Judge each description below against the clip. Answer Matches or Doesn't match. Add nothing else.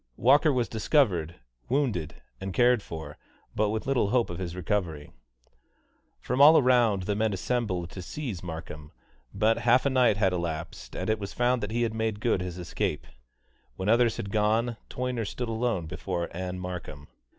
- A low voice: Matches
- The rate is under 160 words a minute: Doesn't match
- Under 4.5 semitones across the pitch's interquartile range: Doesn't match